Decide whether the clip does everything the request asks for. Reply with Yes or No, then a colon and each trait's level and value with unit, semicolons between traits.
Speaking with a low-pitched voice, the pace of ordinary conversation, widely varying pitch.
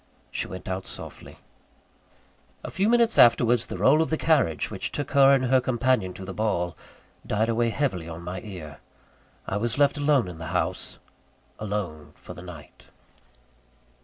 Yes: low, 110 Hz; average, 165 wpm; wide, 7.0 semitones